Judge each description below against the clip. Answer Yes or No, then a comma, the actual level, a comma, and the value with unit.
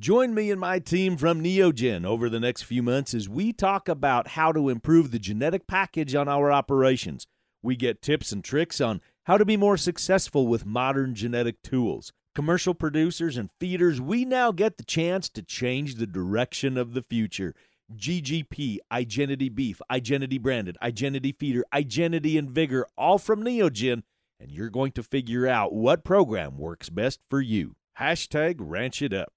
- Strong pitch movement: Yes, wide, 5.7 semitones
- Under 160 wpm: No, average, 170 wpm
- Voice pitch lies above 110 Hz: Yes, medium, 140 Hz